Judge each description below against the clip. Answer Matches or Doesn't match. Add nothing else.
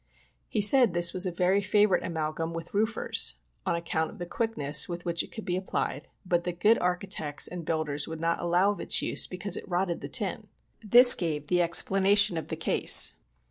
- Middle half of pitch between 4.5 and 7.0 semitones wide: Doesn't match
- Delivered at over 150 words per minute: Matches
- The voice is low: Doesn't match